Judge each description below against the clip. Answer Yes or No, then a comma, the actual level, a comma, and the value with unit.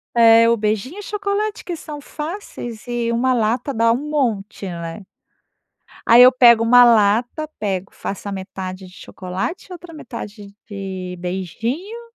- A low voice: No, high, 230 Hz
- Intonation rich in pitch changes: Yes, wide, 6.5 semitones